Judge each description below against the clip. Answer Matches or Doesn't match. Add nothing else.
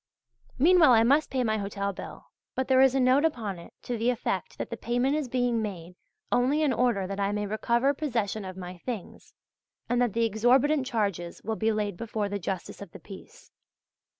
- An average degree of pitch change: Matches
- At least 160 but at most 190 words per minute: Doesn't match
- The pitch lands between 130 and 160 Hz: Doesn't match